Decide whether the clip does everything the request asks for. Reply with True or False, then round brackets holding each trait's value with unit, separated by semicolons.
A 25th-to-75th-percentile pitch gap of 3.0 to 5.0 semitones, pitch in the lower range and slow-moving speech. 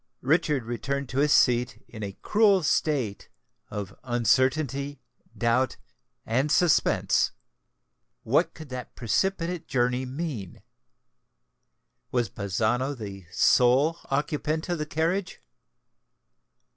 True (4.6 semitones; 130 Hz; 100 wpm)